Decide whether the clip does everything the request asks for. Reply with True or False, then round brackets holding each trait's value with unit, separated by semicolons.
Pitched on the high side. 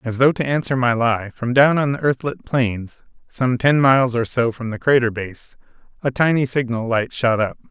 False (125 Hz)